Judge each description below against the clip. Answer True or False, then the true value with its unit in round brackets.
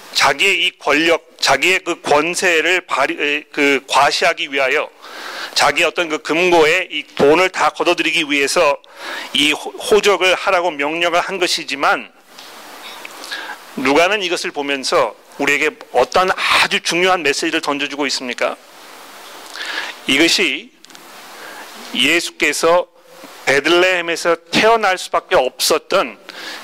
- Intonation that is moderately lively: True (3.7 semitones)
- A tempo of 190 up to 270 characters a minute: True (250 characters per minute)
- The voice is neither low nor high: True (170 Hz)